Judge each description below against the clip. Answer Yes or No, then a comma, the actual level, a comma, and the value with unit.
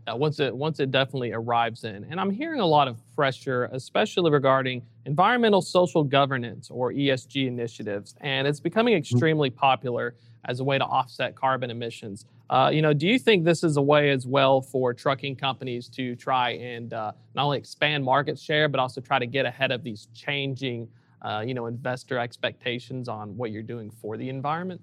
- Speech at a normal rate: Yes, average, 195 wpm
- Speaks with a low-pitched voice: Yes, low, 130 Hz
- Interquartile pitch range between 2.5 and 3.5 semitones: Yes, average, 3.2 semitones